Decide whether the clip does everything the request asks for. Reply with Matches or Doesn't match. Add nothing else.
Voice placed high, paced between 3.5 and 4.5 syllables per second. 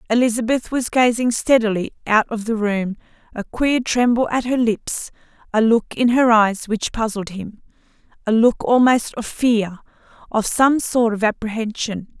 Matches